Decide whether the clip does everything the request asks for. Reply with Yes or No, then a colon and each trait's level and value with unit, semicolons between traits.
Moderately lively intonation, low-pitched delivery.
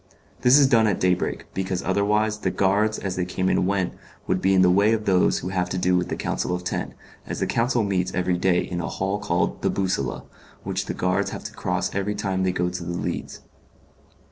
No: narrow, 2.1 semitones; very low, 95 Hz